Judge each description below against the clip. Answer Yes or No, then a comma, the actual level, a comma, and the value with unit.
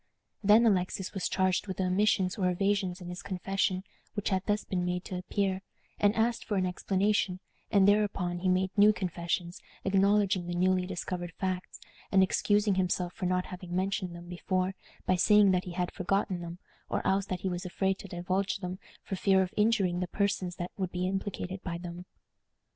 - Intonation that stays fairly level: Yes, narrow, 1.7 semitones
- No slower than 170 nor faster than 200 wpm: Yes, average, 190 wpm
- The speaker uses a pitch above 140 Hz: Yes, medium, 185 Hz